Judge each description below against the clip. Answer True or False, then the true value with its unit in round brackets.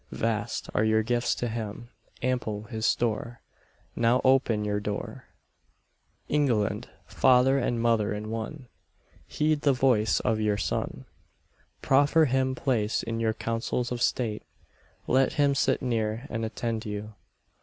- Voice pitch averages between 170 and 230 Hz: False (115 Hz)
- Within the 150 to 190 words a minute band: False (135 wpm)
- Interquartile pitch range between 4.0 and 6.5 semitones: False (2.9 semitones)